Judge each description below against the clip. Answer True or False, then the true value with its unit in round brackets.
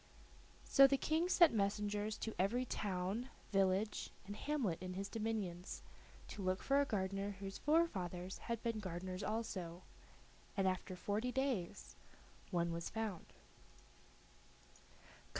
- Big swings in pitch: False (3.7 semitones)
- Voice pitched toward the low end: False (205 Hz)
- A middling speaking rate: False (125 wpm)